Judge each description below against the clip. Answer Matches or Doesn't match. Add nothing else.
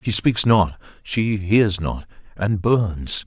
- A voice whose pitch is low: Matches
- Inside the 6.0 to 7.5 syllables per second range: Doesn't match